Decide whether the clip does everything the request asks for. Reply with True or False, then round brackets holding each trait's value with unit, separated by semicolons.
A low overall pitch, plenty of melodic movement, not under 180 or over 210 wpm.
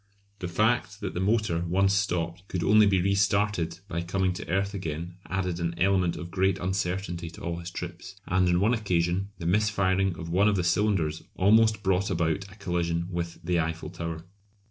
False (90 Hz; 2.5 semitones; 190 wpm)